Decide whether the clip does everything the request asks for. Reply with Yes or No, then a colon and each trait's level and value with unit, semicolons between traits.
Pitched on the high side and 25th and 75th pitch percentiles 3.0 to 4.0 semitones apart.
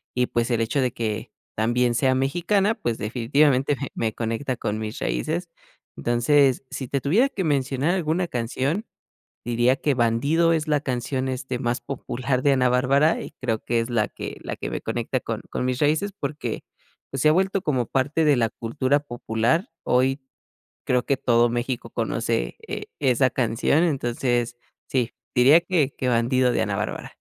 No: low, 130 Hz; average, 3.5 semitones